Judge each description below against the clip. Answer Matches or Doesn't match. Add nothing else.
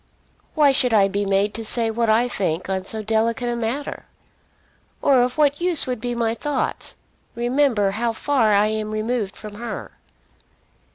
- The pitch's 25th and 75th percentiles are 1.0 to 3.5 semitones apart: Matches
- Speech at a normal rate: Matches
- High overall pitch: Matches